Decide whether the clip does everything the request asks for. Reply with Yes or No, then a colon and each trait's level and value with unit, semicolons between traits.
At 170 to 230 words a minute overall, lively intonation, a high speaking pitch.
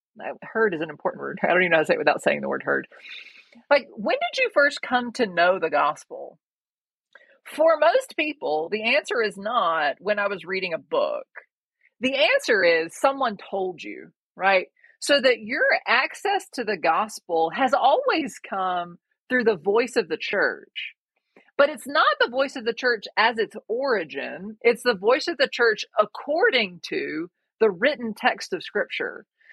Yes: average, 180 wpm; wide, 8.6 semitones; very high, 255 Hz